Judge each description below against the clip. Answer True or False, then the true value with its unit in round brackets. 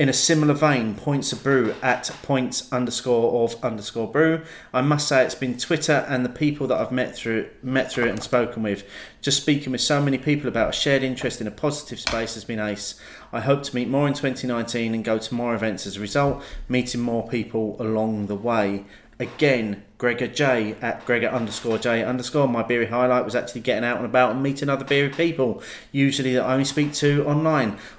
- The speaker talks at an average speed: False (210 wpm)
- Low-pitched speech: True (125 Hz)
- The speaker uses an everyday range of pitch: True (3.3 semitones)